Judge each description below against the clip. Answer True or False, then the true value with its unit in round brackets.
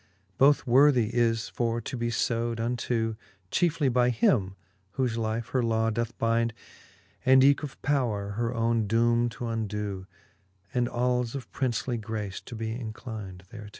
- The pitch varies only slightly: True (1.8 semitones)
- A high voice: False (115 Hz)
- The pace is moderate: True (150 wpm)